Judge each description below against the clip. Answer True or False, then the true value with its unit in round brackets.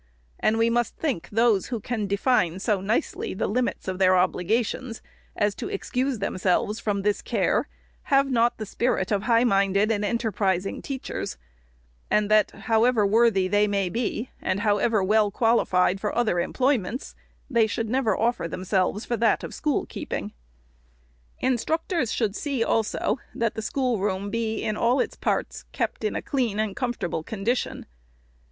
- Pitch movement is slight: False (3.3 semitones)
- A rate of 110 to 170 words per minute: True (165 wpm)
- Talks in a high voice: True (220 Hz)